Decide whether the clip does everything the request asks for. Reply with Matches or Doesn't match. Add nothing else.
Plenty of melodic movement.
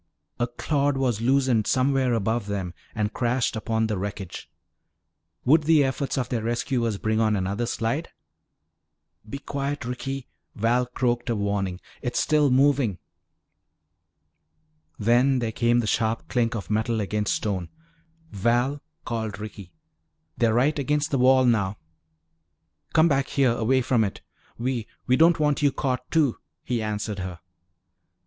Doesn't match